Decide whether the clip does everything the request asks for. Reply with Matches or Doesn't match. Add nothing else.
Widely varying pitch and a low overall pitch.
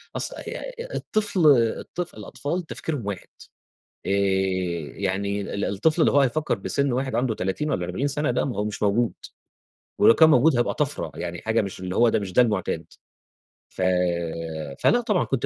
Matches